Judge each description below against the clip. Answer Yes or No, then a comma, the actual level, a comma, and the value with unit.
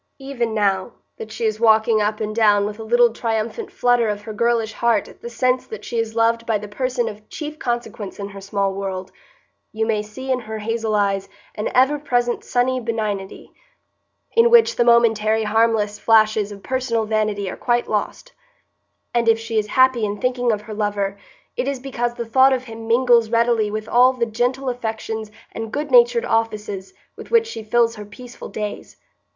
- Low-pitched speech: No, high, 225 Hz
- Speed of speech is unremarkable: Yes, average, 190 wpm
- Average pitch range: No, narrow, 2.3 semitones